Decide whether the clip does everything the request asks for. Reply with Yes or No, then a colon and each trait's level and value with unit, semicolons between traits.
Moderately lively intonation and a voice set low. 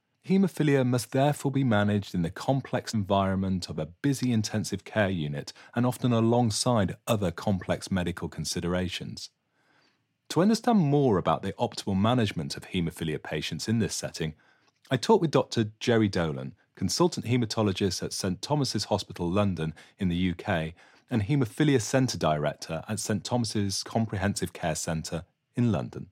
No: wide, 5.9 semitones; low, 105 Hz